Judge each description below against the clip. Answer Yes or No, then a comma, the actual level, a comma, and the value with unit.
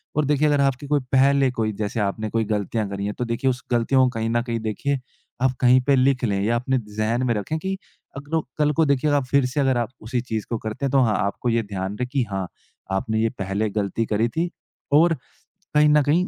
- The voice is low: Yes, low, 125 Hz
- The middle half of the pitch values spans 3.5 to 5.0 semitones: Yes, average, 4.2 semitones